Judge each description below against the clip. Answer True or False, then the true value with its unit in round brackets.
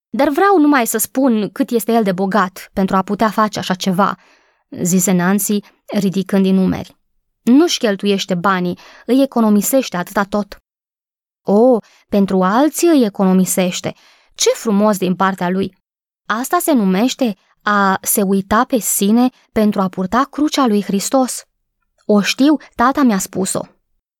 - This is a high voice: True (210 Hz)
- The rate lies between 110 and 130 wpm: False (140 wpm)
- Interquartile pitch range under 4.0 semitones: False (4.6 semitones)